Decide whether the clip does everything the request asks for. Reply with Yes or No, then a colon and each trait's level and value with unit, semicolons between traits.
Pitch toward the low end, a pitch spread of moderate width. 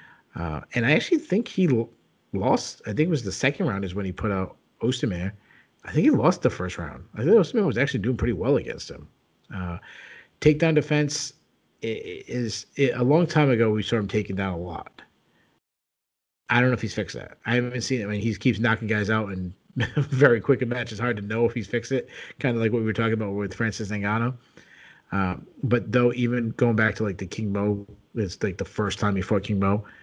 Yes: low, 115 Hz; average, 3.7 semitones